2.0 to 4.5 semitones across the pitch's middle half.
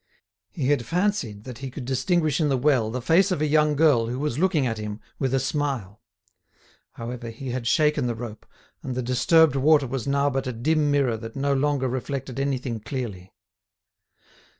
Yes: average, 3.6 semitones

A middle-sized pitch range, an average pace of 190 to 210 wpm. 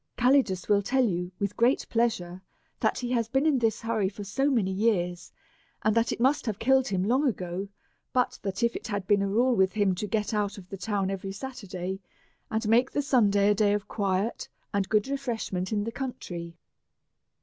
Yes: average, 3.8 semitones; fast, 205 wpm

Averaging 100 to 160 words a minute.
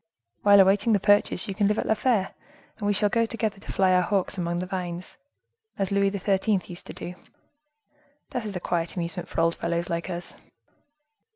No: average, 200 wpm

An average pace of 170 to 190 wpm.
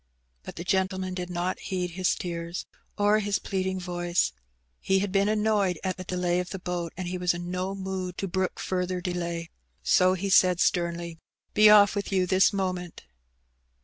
Yes: average, 180 wpm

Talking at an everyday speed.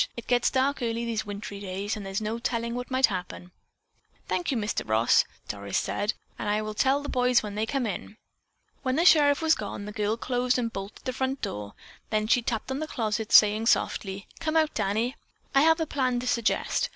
No: fast, 210 wpm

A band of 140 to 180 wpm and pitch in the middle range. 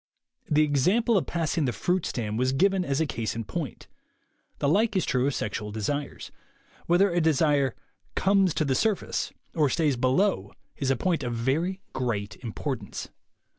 Yes: average, 170 wpm; medium, 145 Hz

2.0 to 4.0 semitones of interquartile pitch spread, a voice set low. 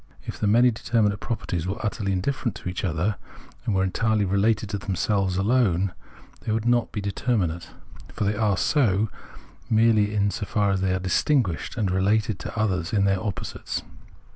Yes: average, 2.8 semitones; low, 100 Hz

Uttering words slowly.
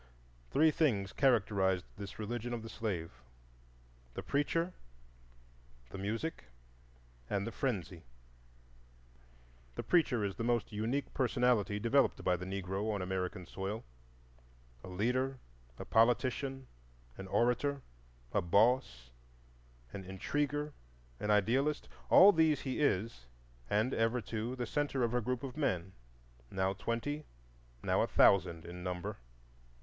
Yes: slow, 120 wpm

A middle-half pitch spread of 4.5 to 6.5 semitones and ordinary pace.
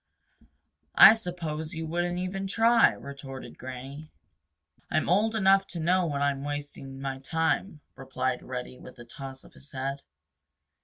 Yes: average, 5.0 semitones; average, 145 wpm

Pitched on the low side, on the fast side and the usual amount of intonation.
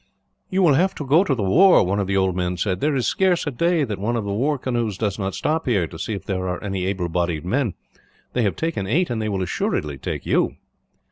No: low, 105 Hz; fast, 260 wpm; wide, 7.3 semitones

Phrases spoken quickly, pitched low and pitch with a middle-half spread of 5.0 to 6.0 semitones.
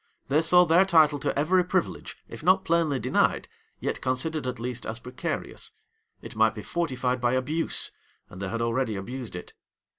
No: average, 175 wpm; low, 130 Hz; wide, 5.6 semitones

